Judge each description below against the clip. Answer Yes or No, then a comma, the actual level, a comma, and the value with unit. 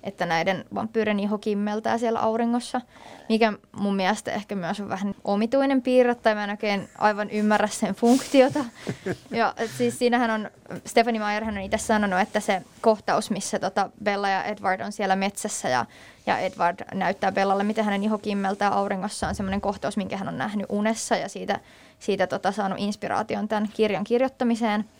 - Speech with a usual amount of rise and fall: No, narrow, 2.1 semitones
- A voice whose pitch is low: No, high, 210 Hz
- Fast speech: Yes, fast, 175 wpm